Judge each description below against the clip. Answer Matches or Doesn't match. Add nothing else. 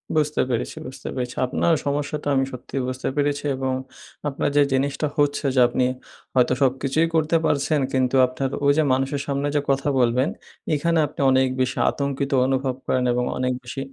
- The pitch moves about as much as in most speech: Doesn't match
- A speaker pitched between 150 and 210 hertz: Doesn't match